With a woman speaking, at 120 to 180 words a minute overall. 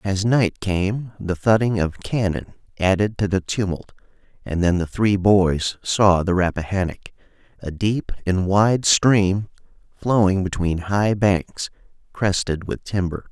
No: male; average, 140 wpm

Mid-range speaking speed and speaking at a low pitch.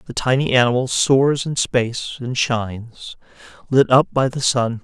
Yes: average, 160 wpm; low, 125 Hz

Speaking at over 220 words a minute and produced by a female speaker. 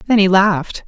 No: fast, 205 wpm; female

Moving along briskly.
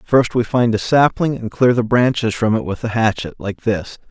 Yes: fast, 220 wpm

